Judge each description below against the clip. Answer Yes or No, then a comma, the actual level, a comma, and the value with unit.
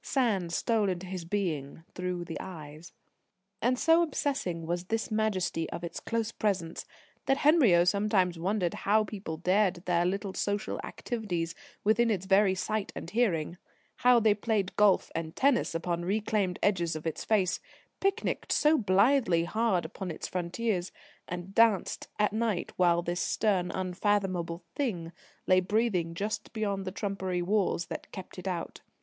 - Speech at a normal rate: Yes, average, 155 wpm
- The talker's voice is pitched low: No, high, 190 Hz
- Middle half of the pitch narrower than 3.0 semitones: No, average, 3.8 semitones